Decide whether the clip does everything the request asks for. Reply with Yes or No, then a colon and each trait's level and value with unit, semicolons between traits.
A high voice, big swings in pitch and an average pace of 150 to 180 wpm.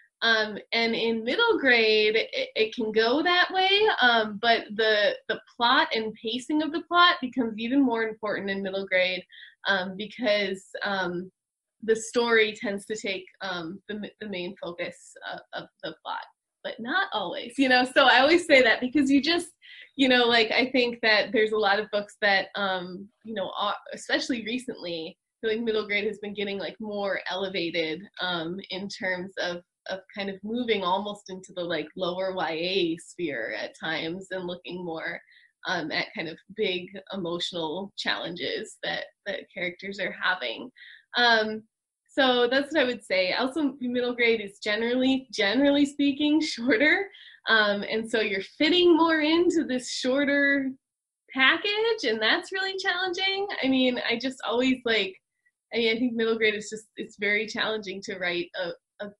Yes: high, 225 Hz; wide, 6.2 semitones; average, 170 wpm